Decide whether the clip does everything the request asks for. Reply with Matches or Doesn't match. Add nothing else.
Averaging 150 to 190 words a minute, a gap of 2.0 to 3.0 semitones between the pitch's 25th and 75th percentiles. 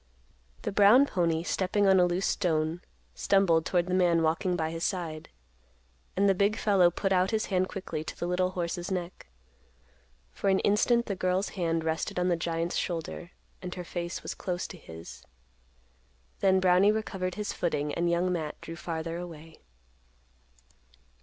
Matches